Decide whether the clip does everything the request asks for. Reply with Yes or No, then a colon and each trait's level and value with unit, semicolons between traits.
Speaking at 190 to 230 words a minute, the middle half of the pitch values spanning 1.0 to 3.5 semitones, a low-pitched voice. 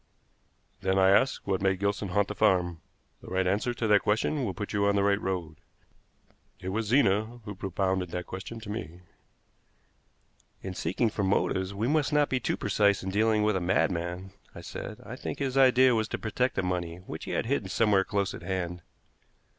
Yes: average, 200 wpm; average, 2.7 semitones; low, 100 Hz